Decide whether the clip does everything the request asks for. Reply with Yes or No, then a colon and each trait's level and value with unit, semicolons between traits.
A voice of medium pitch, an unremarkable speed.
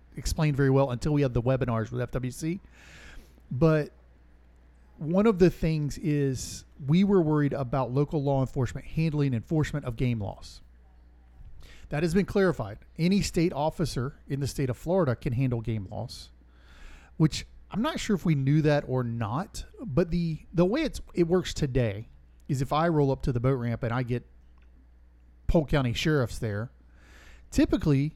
No: low, 130 Hz; average, 170 wpm